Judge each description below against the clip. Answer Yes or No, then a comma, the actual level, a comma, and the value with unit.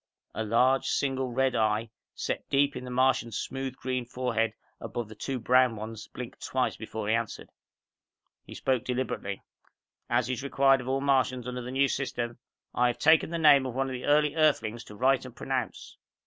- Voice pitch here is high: No, low, 125 Hz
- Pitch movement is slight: Yes, narrow, 2.3 semitones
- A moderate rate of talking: Yes, average, 190 wpm